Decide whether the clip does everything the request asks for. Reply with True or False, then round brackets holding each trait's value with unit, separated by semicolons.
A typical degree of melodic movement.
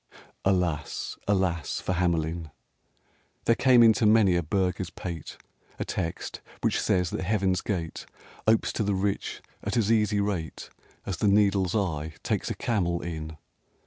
True (3.4 semitones)